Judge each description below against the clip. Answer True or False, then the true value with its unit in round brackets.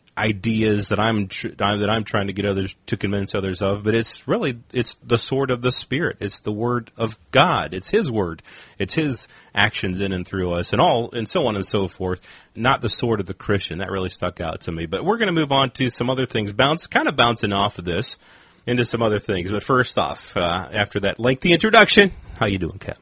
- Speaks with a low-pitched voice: True (110 Hz)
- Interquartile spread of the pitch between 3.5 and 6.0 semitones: True (3.9 semitones)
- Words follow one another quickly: True (235 wpm)